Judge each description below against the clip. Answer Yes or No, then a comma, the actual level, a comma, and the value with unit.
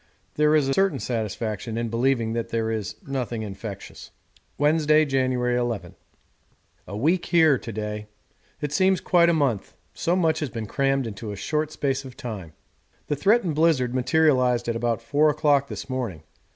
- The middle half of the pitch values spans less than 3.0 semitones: No, average, 4.9 semitones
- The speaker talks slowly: No, average, 165 wpm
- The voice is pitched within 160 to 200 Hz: No, low, 130 Hz